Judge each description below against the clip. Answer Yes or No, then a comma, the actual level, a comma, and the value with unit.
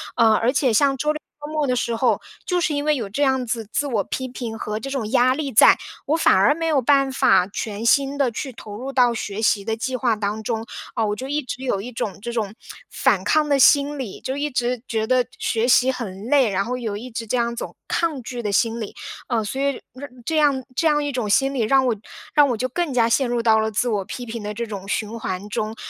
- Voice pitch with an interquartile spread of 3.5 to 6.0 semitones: Yes, average, 3.8 semitones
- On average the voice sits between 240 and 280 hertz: Yes, high, 245 Hz